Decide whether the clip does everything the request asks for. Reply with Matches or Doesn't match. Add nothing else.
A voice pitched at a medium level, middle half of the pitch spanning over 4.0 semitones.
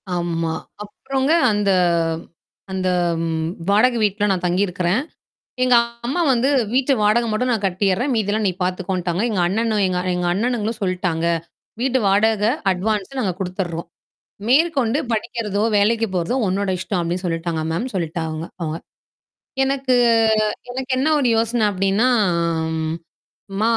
Doesn't match